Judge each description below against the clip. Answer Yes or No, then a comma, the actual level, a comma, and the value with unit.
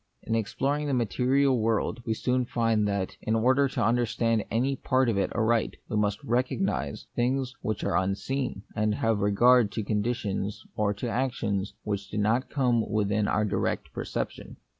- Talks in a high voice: No, low, 115 Hz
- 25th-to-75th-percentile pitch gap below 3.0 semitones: No, average, 3.3 semitones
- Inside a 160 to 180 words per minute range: Yes, average, 165 wpm